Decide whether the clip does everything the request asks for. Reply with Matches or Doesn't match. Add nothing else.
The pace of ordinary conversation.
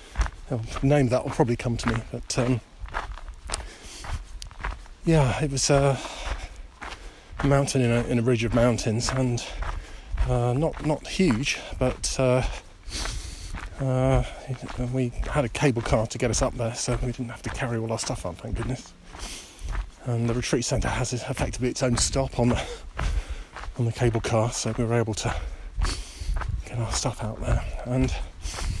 Matches